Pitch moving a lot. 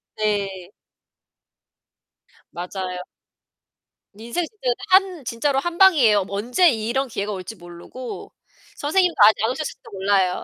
Yes: wide, 6.5 semitones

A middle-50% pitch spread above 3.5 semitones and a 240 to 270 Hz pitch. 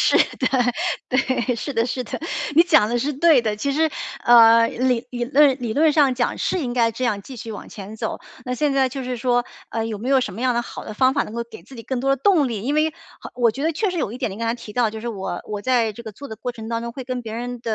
No: average, 2.8 semitones; high, 245 Hz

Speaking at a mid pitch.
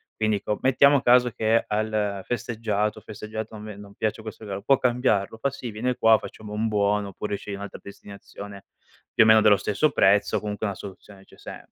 No: low, 105 Hz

